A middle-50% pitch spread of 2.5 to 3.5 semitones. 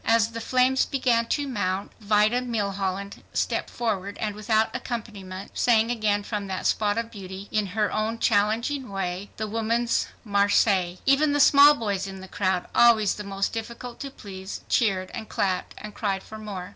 Yes: average, 2.9 semitones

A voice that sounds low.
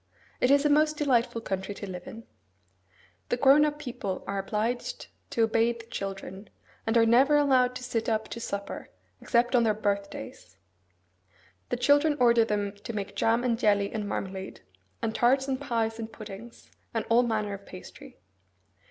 No: high, 230 Hz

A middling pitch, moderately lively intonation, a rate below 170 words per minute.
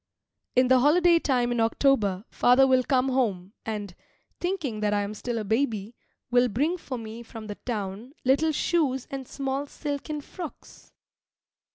No: very high, 255 Hz; average, 4.3 semitones; average, 160 wpm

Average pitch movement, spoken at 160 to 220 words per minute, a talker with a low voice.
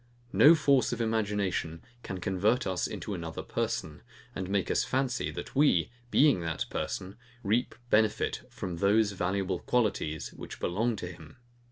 No: average, 4.5 semitones; average, 150 wpm; low, 100 Hz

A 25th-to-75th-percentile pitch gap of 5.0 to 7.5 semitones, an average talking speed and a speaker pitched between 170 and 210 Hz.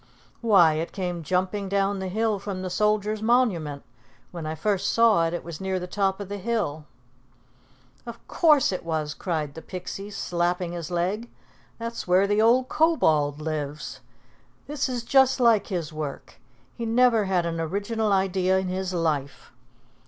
No: average, 4.4 semitones; average, 165 wpm; high, 190 Hz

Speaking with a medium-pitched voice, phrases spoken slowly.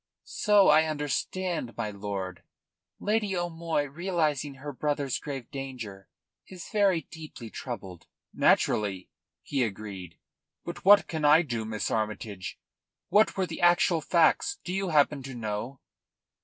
Yes: medium, 145 Hz; slow, 130 wpm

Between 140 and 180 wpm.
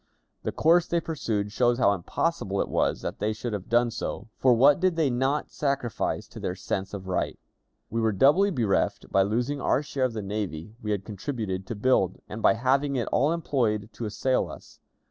No: fast, 205 wpm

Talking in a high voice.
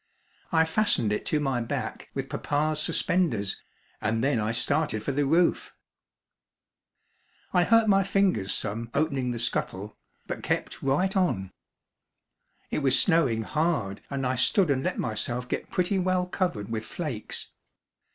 No: medium, 140 Hz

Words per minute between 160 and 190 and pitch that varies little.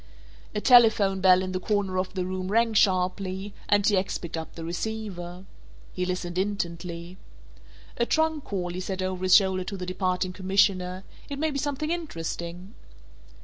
Yes: average, 170 wpm; narrow, 2.3 semitones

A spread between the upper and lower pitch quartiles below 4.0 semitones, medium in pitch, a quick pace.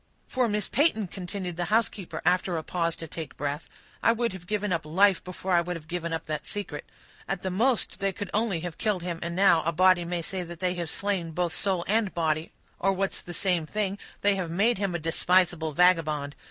Yes: average, 2.9 semitones; medium, 180 Hz; fast, 220 wpm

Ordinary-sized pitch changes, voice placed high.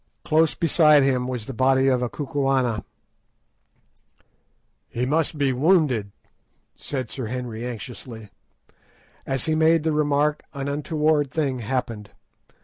No: average, 3.4 semitones; low, 135 Hz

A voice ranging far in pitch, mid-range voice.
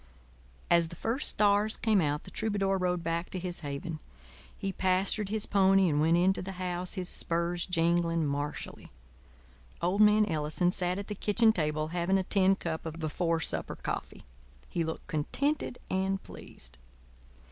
No: average, 2.8 semitones; medium, 180 Hz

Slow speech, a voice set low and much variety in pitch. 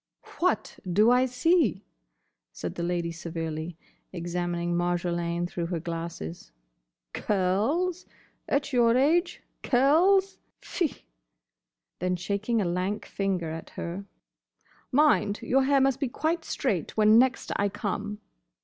No: slow, 120 wpm; high, 200 Hz; wide, 7.4 semitones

